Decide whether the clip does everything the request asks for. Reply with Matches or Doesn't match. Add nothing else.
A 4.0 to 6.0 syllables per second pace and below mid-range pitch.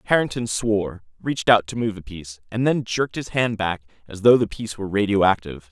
Doesn't match